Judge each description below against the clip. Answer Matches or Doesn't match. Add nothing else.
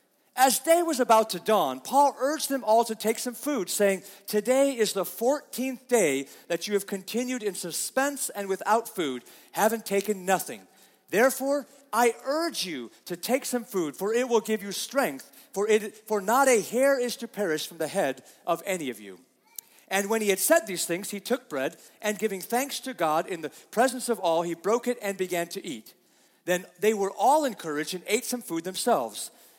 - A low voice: Doesn't match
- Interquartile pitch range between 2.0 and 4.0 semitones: Doesn't match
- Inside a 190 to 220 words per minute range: Matches